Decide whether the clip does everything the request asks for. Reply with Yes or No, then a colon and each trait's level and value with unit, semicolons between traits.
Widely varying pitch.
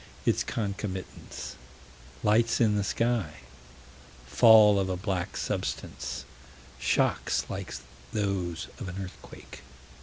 No: average, 2.9 semitones